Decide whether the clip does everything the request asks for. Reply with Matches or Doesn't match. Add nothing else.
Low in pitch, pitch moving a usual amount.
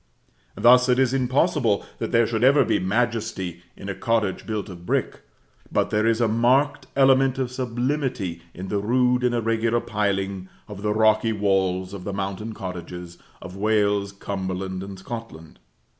Matches